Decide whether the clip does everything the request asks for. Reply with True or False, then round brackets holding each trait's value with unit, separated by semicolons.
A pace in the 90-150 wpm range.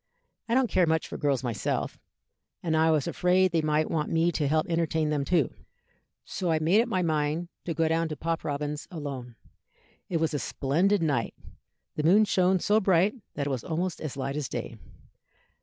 False (195 wpm)